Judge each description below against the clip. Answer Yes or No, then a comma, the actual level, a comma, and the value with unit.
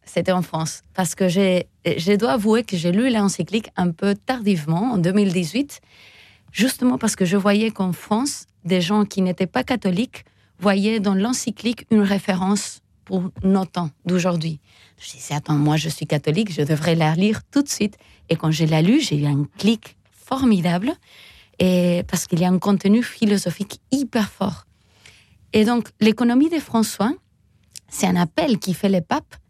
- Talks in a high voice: Yes, high, 195 Hz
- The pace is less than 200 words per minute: Yes, average, 175 wpm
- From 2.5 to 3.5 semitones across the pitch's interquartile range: No, average, 4.0 semitones